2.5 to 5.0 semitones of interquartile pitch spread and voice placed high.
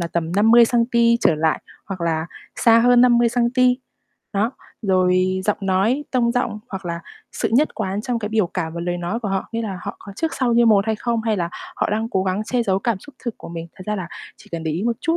Yes: average, 4.3 semitones; high, 210 Hz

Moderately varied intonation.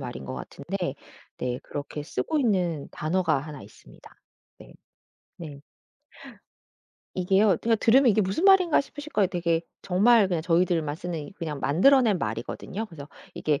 No: wide, 6.0 semitones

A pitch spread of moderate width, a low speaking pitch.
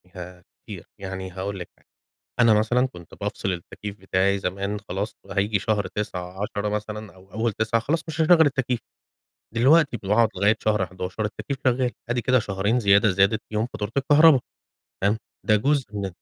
Yes: average, 3.6 semitones; low, 105 Hz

